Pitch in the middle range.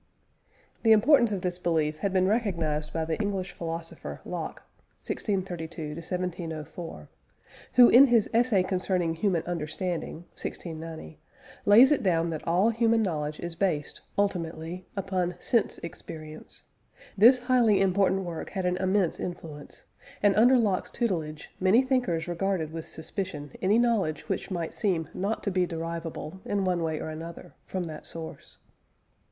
Yes: medium, 180 Hz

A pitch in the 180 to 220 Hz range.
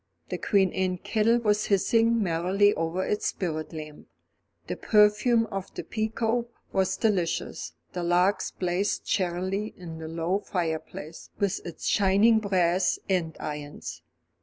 Yes: high, 190 Hz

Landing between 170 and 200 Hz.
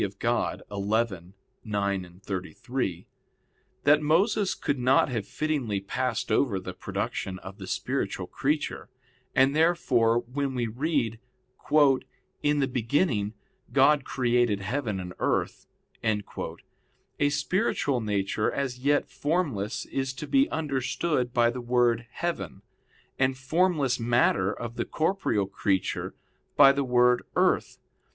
No: low, 125 Hz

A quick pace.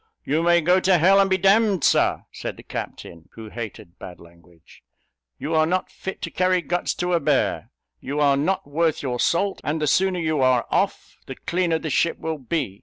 Yes: fast, 210 wpm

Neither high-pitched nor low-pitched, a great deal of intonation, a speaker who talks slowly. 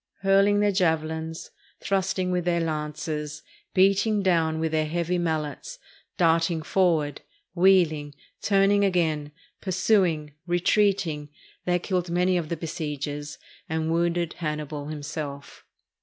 No: medium, 165 Hz; average, 3.2 semitones; slow, 110 wpm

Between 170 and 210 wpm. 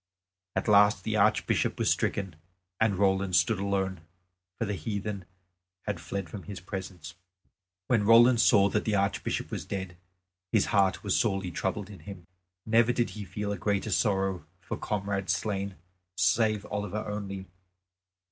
No: average, 150 wpm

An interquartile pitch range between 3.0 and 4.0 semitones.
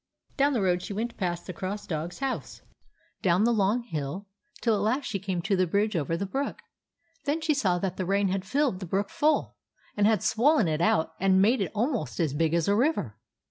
No: average, 4.8 semitones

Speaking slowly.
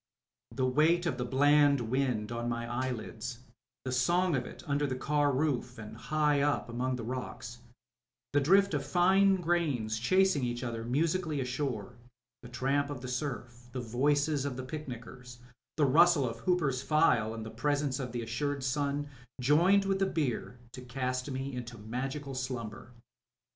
No: average, 165 wpm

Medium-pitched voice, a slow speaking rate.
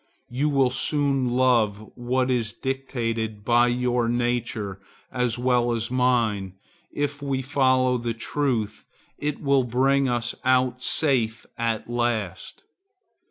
No: low, 125 Hz; slow, 125 wpm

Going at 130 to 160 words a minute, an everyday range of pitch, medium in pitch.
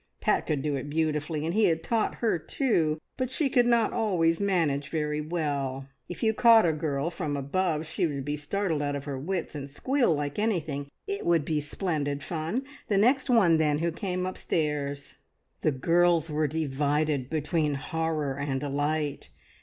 No: average, 175 wpm; average, 3.9 semitones; medium, 155 Hz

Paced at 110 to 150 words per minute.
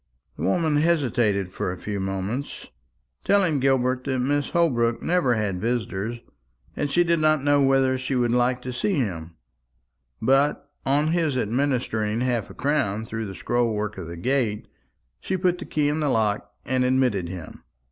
No: average, 170 wpm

